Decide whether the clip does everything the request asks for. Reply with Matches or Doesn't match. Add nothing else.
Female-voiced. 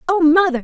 Matches